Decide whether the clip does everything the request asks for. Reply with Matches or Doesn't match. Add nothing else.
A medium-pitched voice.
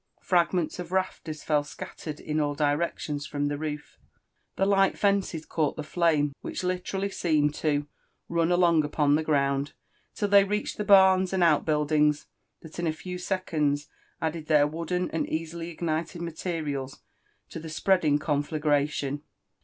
Matches